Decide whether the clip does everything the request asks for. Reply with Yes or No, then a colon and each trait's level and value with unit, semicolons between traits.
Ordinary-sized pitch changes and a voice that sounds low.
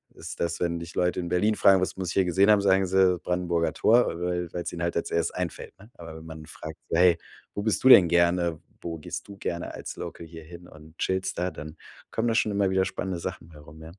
No: narrow, 2.2 semitones; very low, 90 Hz